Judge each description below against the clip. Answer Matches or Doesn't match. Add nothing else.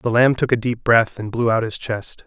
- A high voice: Doesn't match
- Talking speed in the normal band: Doesn't match